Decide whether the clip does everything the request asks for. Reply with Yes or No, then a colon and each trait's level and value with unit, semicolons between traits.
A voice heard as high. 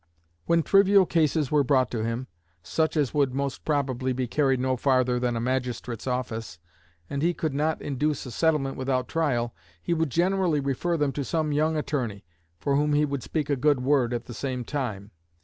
No: medium, 140 Hz